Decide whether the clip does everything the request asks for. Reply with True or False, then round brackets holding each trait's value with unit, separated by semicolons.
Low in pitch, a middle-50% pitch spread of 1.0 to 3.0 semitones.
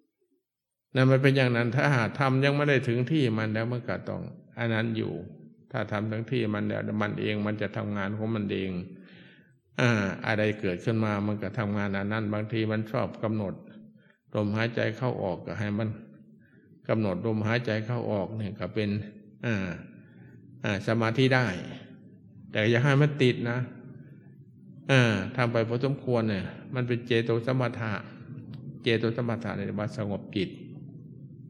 False (115 Hz; 3.4 semitones)